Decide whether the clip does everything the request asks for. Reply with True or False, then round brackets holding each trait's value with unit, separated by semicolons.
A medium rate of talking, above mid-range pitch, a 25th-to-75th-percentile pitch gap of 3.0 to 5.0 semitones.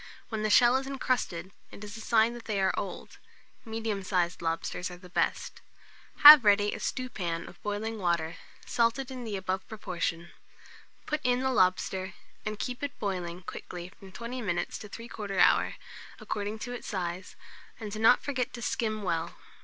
True (170 wpm; 210 Hz; 4.4 semitones)